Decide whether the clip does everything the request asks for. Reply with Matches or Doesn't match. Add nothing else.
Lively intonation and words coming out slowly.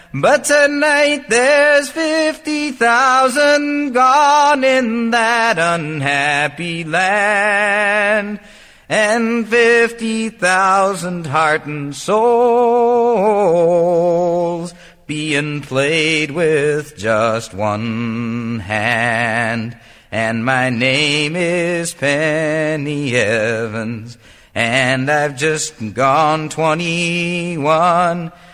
Matches